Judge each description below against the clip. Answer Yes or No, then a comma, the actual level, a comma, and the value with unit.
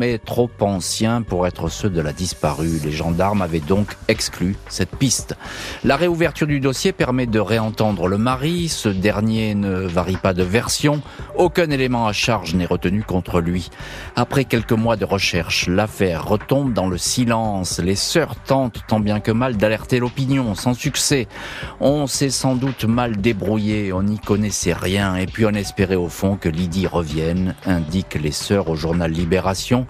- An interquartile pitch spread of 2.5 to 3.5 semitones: No, average, 4.7 semitones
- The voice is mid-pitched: No, low, 105 Hz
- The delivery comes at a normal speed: Yes, average, 175 wpm